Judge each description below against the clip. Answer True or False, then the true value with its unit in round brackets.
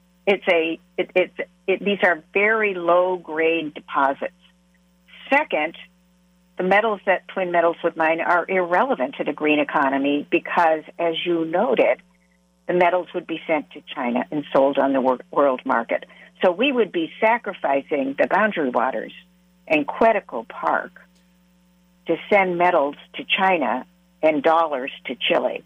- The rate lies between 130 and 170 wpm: True (145 wpm)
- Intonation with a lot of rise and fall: False (2.7 semitones)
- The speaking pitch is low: False (180 Hz)